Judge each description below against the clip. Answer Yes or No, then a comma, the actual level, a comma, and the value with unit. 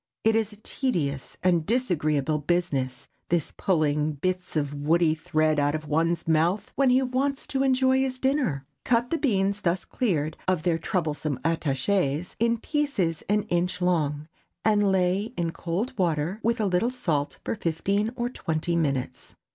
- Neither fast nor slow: Yes, average, 160 wpm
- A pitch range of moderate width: No, wide, 6.2 semitones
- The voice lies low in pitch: No, medium, 180 Hz